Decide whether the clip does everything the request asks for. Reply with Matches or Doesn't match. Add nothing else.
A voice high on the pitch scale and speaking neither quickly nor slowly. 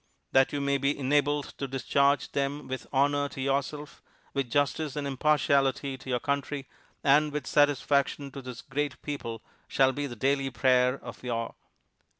Doesn't match